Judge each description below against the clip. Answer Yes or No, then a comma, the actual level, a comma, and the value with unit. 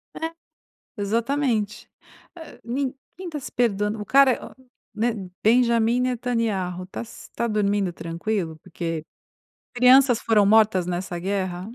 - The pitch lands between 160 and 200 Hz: No, high, 215 Hz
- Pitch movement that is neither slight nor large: Yes, average, 4.5 semitones